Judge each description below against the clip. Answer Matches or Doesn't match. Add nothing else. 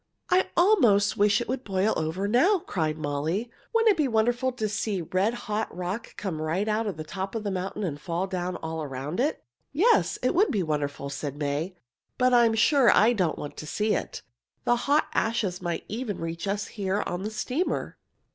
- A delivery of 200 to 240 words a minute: Matches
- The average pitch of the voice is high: Matches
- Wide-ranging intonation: Matches